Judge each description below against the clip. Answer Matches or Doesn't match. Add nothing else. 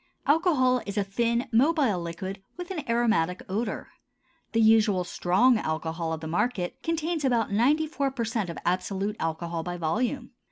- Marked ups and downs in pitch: Matches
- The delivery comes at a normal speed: Matches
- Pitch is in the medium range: Doesn't match